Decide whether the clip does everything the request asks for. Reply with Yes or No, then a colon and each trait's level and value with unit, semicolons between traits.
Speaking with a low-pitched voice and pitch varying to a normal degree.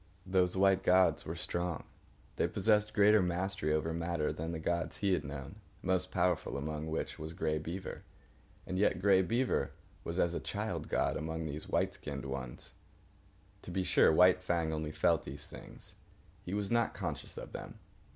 Yes: very low, 85 Hz; average, 3.2 semitones